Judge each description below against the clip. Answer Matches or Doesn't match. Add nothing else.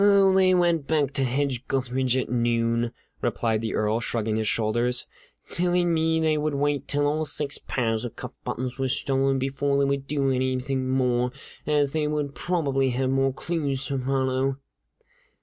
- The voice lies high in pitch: Doesn't match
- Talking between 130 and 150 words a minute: Doesn't match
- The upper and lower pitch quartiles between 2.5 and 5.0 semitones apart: Matches